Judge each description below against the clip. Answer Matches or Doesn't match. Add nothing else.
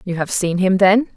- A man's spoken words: Doesn't match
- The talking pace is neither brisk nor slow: Doesn't match